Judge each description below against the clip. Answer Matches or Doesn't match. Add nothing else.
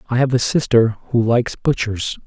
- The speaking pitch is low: Matches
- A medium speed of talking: Matches